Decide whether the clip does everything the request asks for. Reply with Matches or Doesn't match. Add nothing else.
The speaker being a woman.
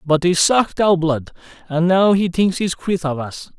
Doesn't match